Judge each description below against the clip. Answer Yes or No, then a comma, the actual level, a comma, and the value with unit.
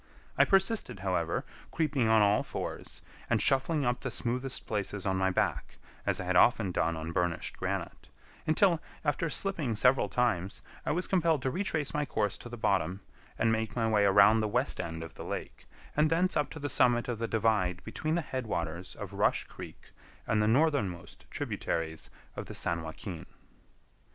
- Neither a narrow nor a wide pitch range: No, wide, 7.2 semitones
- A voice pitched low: Yes, low, 110 Hz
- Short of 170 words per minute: No, average, 185 wpm